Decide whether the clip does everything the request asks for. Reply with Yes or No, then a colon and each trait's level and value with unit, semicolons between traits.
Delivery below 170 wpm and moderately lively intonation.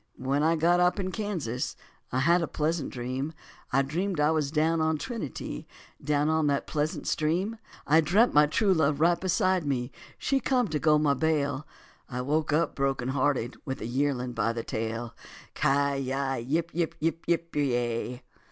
No: average, 180 wpm; average, 3.8 semitones